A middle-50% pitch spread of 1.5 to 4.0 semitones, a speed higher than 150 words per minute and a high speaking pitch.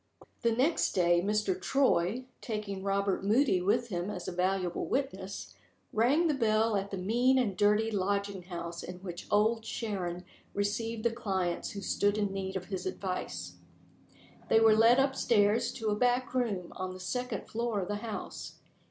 Yes: average, 3.6 semitones; average, 170 wpm; high, 205 Hz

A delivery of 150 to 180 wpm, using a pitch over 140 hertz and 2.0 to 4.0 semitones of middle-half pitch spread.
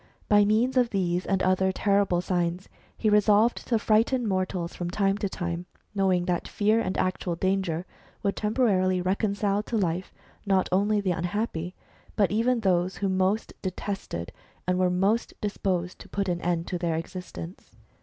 Yes: average, 165 wpm; high, 190 Hz; narrow, 2.6 semitones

